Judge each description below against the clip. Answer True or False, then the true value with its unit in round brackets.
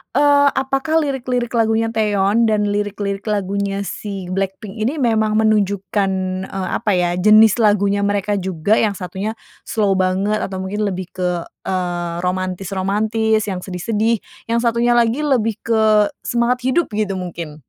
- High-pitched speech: True (205 Hz)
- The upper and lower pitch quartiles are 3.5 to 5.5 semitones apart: False (2.9 semitones)